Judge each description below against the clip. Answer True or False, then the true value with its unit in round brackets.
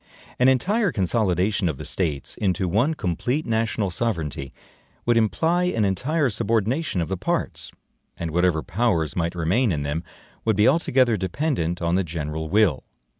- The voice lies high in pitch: False (95 Hz)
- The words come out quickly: False (155 wpm)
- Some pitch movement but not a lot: False (6.3 semitones)